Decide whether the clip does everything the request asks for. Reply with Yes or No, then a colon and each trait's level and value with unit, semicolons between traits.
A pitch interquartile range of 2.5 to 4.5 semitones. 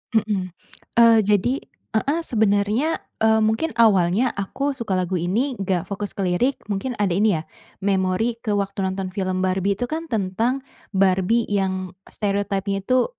Yes: average, 3.1 semitones